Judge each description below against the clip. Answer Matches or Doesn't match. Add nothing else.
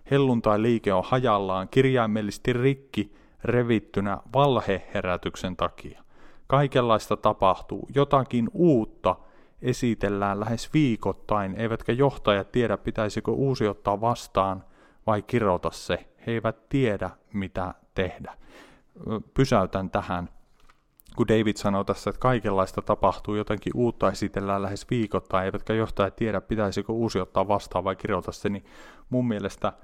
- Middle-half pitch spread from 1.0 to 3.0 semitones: Doesn't match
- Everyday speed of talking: Matches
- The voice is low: Matches